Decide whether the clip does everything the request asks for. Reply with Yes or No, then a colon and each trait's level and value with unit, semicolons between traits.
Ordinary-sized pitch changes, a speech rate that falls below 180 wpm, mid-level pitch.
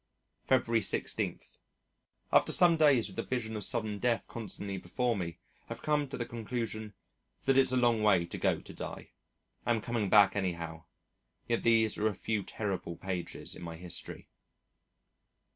No: average, 3.8 semitones; average, 160 wpm; low, 110 Hz